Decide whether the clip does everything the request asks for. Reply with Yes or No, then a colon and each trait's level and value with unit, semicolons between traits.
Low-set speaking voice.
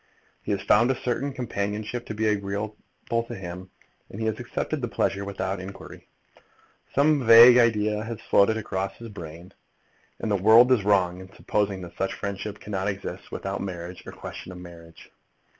Yes: low, 105 Hz